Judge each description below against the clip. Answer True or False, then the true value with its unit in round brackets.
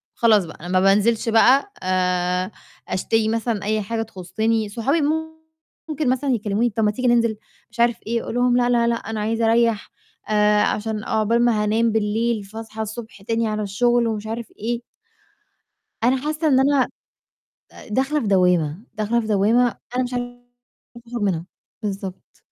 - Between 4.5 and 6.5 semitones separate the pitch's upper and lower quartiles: False (2.4 semitones)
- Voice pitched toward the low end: False (225 Hz)